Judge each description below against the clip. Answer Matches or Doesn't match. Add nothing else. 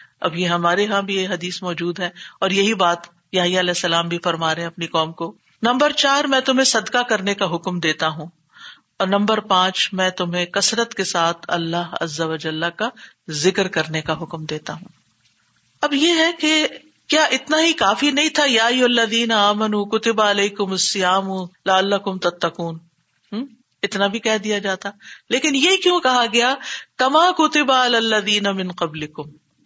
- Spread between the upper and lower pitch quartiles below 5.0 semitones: Doesn't match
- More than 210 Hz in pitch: Doesn't match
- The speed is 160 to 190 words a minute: Matches